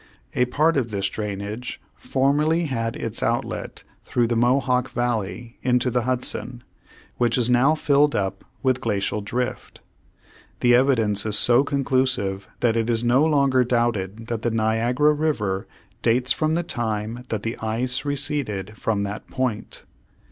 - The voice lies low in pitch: Yes, low, 120 Hz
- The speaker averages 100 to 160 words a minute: Yes, average, 150 wpm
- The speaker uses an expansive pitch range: No, average, 3.1 semitones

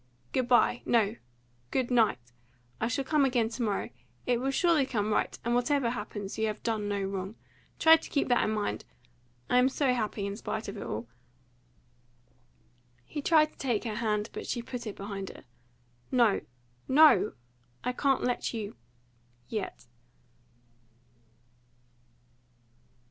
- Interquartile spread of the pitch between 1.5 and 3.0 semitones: No, average, 3.7 semitones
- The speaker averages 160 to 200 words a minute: No, average, 150 wpm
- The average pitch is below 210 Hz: No, high, 235 Hz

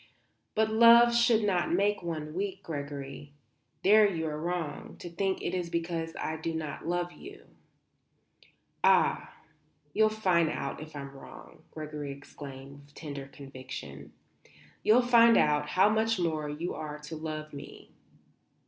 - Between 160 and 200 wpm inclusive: No, average, 145 wpm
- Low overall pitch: No, medium, 165 Hz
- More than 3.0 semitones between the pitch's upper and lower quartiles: Yes, average, 5.2 semitones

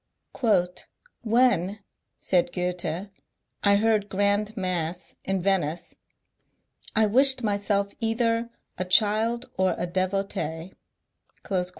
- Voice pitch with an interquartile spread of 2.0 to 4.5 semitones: Yes, average, 3.4 semitones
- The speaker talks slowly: Yes, slow, 100 wpm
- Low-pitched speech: No, high, 200 Hz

